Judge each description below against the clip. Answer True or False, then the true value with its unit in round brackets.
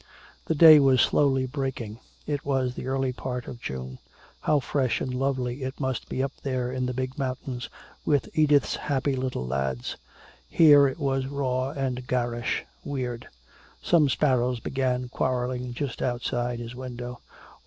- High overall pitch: False (130 Hz)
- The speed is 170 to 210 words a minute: False (155 wpm)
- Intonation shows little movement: True (1.8 semitones)